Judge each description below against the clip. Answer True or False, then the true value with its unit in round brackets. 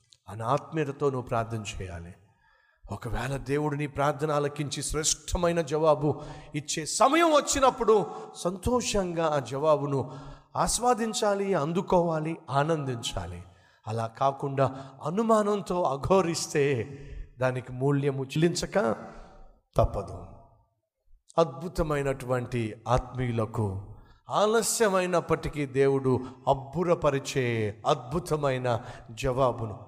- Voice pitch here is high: False (140 Hz)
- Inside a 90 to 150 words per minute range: False (70 wpm)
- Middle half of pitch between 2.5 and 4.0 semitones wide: False (5.1 semitones)